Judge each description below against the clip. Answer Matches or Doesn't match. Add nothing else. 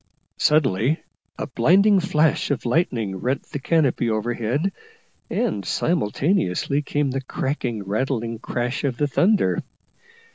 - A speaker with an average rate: Doesn't match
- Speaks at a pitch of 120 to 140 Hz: Matches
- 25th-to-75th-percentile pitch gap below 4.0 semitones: Doesn't match